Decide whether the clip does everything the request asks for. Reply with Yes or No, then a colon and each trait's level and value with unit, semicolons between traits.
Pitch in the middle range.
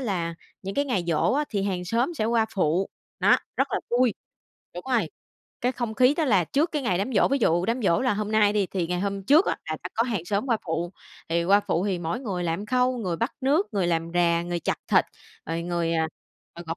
No: high, 200 Hz